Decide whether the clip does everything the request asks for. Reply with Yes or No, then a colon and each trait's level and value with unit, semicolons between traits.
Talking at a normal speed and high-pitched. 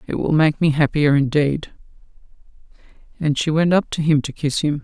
No: average, 185 wpm; medium, 150 Hz